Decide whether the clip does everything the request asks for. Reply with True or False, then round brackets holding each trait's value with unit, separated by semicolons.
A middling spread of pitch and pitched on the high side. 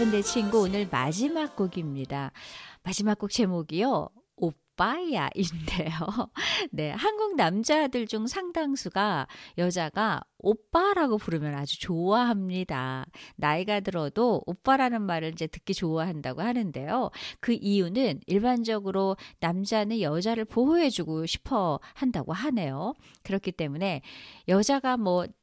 False (5.7 semitones; 195 Hz)